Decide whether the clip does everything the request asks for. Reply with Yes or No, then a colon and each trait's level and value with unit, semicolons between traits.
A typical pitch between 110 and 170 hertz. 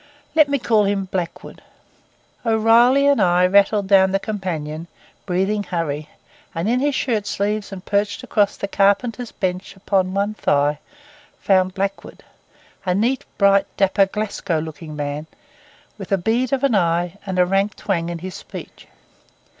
No: high, 195 Hz